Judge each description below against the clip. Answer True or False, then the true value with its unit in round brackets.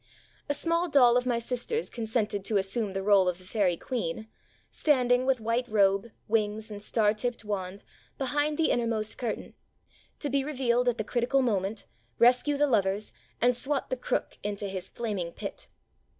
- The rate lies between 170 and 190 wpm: True (175 wpm)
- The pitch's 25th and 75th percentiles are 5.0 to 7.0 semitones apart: False (3.7 semitones)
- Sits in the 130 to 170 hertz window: False (230 Hz)